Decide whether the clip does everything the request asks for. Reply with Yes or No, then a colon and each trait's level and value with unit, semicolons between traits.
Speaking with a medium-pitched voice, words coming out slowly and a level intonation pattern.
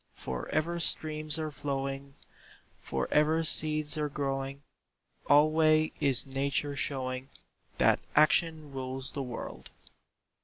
Yes: medium, 145 Hz; slow, 110 wpm; narrow, 2.3 semitones